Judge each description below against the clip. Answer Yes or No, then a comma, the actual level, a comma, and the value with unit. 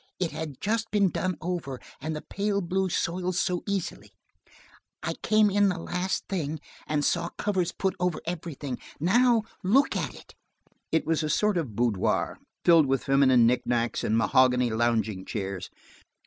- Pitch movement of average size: No, wide, 6.5 semitones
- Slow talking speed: No, average, 160 wpm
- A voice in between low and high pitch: Yes, medium, 165 Hz